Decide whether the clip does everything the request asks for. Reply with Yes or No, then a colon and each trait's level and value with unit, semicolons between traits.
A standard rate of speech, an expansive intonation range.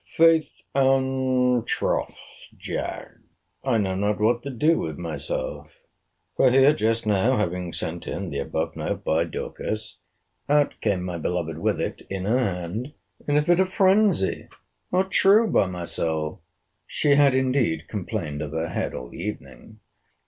Yes: average, 150 wpm; wide, 8.0 semitones